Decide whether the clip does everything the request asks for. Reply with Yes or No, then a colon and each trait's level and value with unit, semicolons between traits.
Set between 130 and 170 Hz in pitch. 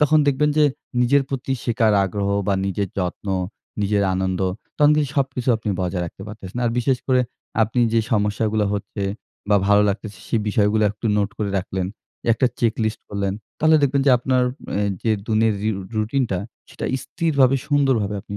No: low, 110 Hz